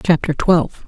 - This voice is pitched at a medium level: Yes, medium, 165 Hz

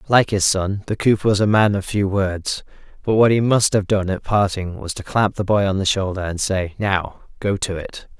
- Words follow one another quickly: Yes, fast, 240 wpm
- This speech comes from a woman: No, male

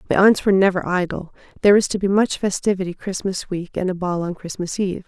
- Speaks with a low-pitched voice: No, medium, 185 Hz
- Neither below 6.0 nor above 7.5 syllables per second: Yes, 6.4 syllables/s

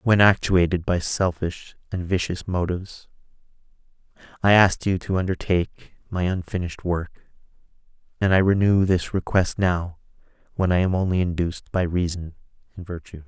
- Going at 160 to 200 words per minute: No, slow, 135 wpm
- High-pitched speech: No, very low, 90 Hz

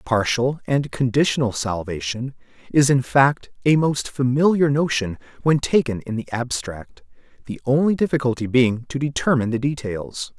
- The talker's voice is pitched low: Yes, low, 130 Hz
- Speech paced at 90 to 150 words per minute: Yes, average, 140 wpm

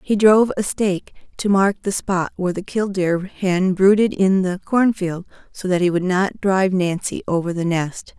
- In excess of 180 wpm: Yes, average, 200 wpm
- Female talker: Yes, female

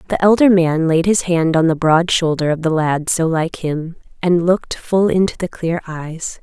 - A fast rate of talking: Yes, fast, 215 wpm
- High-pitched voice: No, medium, 170 Hz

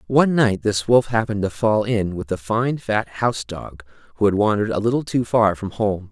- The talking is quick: Yes, fast, 225 wpm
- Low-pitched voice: Yes, low, 105 Hz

